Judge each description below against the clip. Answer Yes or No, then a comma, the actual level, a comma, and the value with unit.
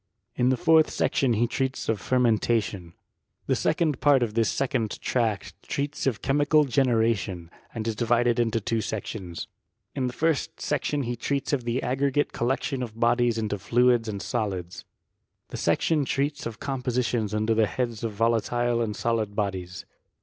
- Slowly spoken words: No, average, 165 wpm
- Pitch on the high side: No, low, 120 Hz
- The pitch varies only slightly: No, average, 3.3 semitones